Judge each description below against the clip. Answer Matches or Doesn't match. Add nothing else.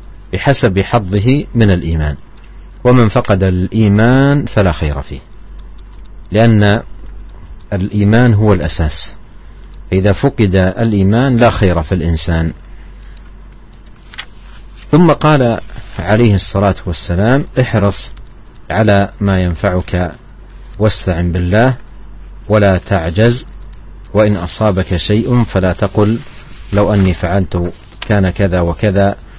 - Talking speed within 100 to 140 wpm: Doesn't match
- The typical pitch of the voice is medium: Doesn't match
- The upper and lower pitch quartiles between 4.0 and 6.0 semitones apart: Doesn't match